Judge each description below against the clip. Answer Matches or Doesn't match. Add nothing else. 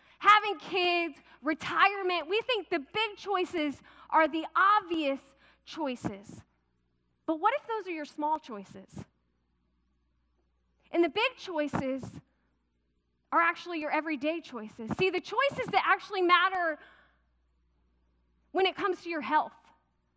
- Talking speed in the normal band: Doesn't match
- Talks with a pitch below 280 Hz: Doesn't match